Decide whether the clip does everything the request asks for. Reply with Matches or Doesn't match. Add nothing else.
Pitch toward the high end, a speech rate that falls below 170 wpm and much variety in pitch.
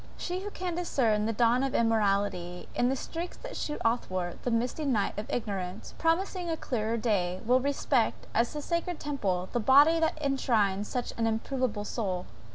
Doesn't match